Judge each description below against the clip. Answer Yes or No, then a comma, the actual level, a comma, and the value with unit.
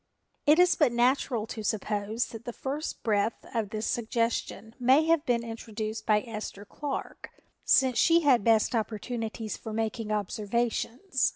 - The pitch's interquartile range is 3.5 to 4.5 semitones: No, average, 2.9 semitones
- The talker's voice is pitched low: No, high, 230 Hz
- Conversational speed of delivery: Yes, average, 150 wpm